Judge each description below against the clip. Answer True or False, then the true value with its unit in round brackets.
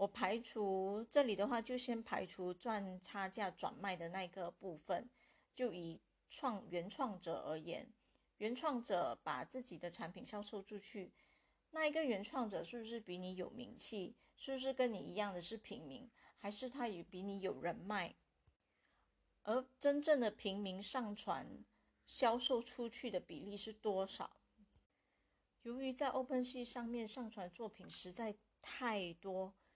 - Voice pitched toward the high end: True (215 Hz)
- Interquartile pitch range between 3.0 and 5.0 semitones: True (4.5 semitones)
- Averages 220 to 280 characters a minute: True (230 characters per minute)